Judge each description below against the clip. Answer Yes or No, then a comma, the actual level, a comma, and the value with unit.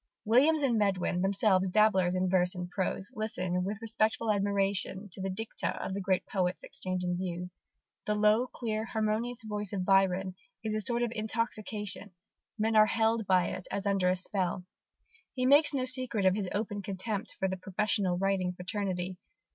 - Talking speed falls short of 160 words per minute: No, average, 170 wpm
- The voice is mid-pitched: No, high, 200 Hz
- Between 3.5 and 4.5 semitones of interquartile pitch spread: No, average, 2.8 semitones